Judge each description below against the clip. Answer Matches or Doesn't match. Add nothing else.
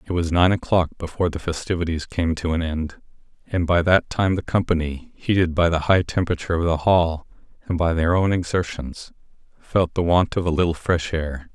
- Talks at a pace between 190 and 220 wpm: Matches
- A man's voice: Matches